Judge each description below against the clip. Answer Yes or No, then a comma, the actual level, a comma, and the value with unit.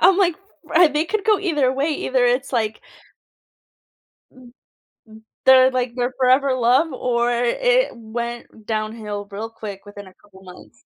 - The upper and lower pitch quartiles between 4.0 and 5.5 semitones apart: Yes, average, 4.6 semitones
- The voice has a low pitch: No, high, 245 Hz